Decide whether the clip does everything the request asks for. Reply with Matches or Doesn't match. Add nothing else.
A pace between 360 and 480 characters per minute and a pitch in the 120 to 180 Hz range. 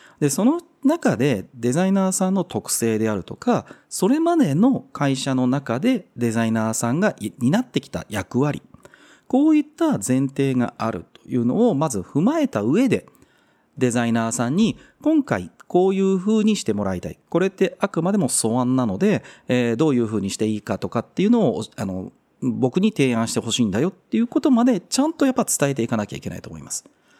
Matches